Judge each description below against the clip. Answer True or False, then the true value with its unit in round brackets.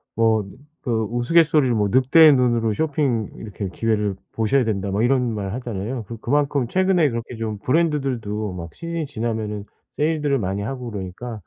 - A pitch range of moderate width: True (4.6 semitones)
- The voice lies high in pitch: False (115 Hz)